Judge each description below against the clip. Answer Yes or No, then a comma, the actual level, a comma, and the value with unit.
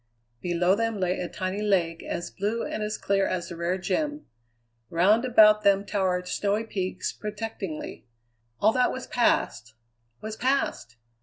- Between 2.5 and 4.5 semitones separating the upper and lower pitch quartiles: Yes, average, 3.2 semitones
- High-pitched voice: Yes, high, 200 Hz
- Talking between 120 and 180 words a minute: Yes, average, 150 wpm